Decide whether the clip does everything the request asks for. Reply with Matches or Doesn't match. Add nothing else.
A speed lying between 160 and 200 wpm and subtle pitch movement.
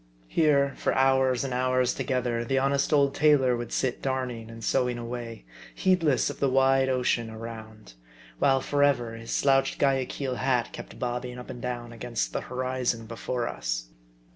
Matches